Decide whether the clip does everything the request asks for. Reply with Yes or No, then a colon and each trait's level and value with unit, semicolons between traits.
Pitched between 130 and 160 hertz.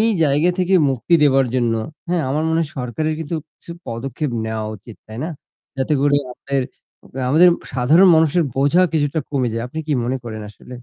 Yes: medium, 140 Hz